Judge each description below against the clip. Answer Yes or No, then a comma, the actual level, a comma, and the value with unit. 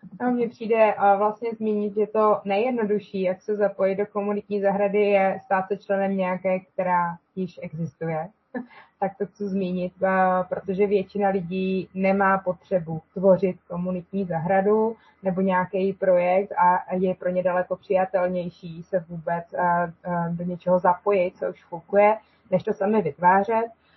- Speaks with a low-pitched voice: No, high, 190 Hz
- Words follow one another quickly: No, average, 135 wpm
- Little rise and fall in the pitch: Yes, narrow, 2.1 semitones